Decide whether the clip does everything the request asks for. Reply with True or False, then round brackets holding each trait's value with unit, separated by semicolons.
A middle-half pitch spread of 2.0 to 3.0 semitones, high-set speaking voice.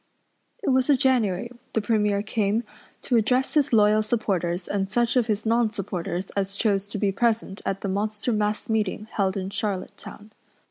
True (2.6 semitones; 210 Hz)